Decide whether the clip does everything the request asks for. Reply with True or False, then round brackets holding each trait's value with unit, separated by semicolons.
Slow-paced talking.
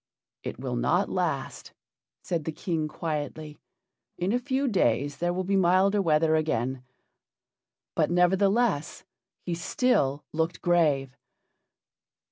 True (115 wpm)